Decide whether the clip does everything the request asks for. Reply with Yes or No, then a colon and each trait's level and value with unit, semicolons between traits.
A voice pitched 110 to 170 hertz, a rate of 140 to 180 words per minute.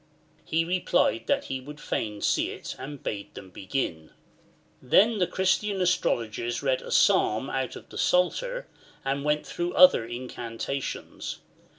Yes: low, 135 Hz; average, 145 wpm